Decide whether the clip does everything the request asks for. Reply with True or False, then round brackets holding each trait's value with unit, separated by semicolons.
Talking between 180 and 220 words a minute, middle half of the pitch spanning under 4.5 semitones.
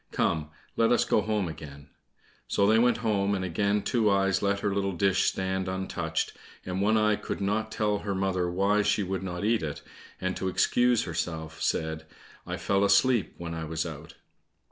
True (190 wpm; 3.0 semitones)